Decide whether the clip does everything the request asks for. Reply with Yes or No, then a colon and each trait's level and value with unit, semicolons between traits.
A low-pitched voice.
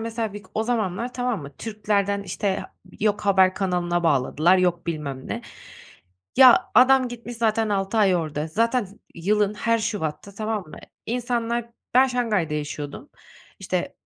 No: high, 205 Hz